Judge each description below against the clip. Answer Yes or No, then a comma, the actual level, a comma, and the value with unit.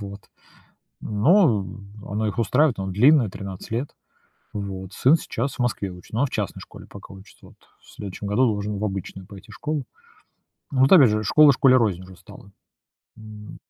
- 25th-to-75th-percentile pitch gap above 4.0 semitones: Yes, average, 4.4 semitones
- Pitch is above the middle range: No, low, 105 Hz